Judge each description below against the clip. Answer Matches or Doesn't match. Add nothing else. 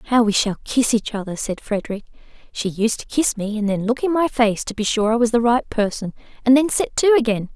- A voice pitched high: Matches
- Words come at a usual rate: Doesn't match